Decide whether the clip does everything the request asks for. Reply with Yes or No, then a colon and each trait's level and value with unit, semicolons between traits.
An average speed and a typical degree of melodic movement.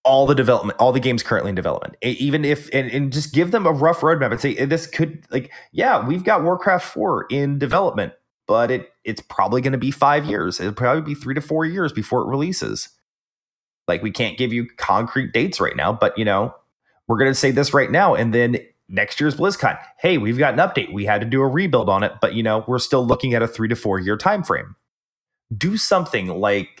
No: fast, 230 wpm; average, 4.6 semitones